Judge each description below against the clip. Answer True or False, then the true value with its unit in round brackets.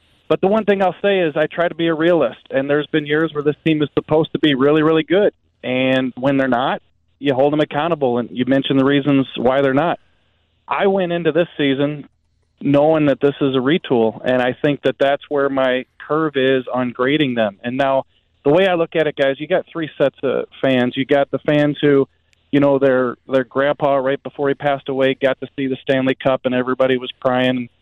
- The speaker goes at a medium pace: False (230 wpm)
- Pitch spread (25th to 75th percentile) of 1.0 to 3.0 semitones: True (2.6 semitones)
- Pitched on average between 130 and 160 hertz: True (140 Hz)